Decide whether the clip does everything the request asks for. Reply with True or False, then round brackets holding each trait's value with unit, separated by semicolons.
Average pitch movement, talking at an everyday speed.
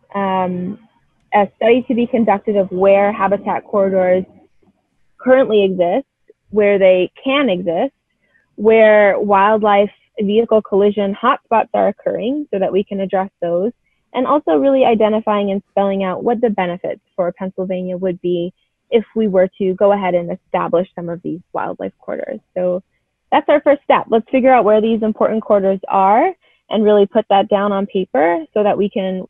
True (3.2 semitones; 165 wpm)